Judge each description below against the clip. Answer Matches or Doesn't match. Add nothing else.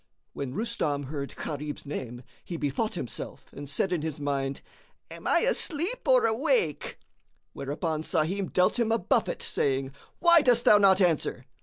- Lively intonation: Matches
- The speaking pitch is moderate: Matches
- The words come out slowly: Doesn't match